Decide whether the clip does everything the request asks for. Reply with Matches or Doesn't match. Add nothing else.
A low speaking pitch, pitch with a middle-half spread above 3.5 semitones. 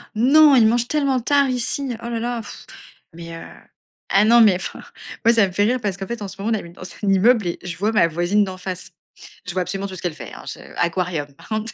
Doesn't match